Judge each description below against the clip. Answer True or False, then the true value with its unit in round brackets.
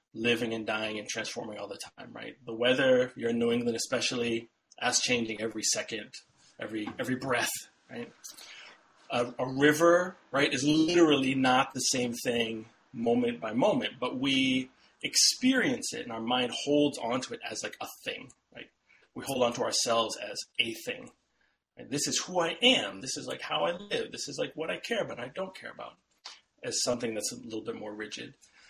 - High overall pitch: False (135 Hz)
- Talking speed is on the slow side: False (190 wpm)